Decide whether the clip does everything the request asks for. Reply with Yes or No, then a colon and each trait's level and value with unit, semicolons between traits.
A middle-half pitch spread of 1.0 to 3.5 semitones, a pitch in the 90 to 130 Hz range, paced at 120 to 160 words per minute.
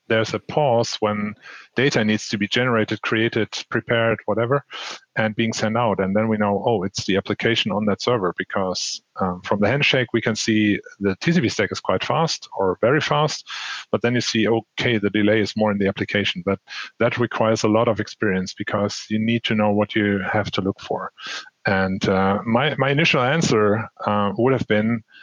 No: narrow, 2.4 semitones; low, 110 Hz; average, 200 wpm